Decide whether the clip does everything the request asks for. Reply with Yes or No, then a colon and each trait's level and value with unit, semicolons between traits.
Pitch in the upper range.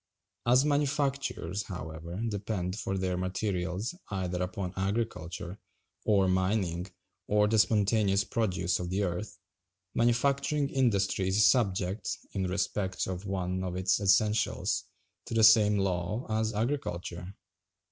No: very low, 95 Hz